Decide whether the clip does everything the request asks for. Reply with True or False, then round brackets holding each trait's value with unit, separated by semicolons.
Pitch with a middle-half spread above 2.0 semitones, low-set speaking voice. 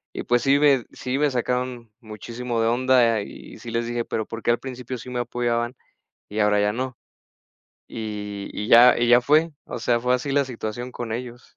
False (1.7 semitones; 120 Hz)